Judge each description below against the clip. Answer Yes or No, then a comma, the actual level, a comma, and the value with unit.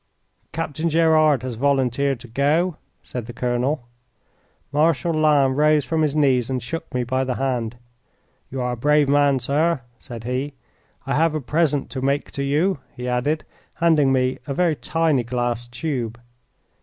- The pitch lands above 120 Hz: Yes, medium, 140 Hz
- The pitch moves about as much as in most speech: Yes, average, 3.6 semitones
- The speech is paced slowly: No, average, 165 wpm